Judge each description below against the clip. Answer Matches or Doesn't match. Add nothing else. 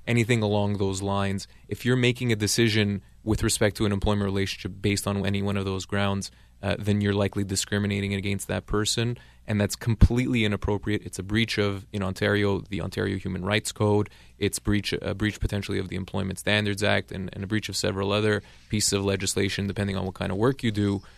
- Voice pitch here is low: Matches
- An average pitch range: Doesn't match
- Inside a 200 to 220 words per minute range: Matches